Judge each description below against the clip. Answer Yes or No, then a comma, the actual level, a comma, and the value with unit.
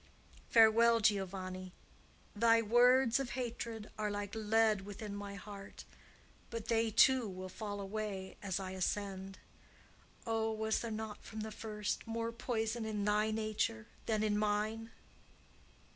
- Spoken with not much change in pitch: Yes, narrow, 1.8 semitones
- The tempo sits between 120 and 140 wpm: Yes, slow, 135 wpm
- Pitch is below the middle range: No, high, 215 Hz